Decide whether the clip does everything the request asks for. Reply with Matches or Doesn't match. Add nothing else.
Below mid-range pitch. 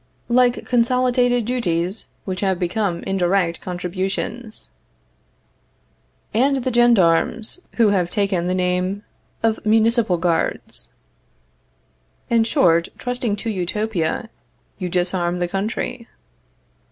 Doesn't match